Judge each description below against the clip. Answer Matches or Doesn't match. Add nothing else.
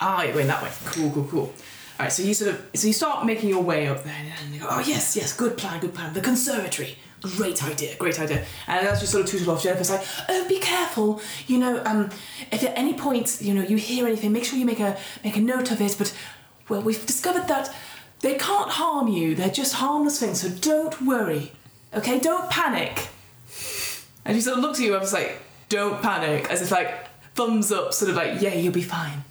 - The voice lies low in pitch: Doesn't match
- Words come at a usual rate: Doesn't match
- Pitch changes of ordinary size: Doesn't match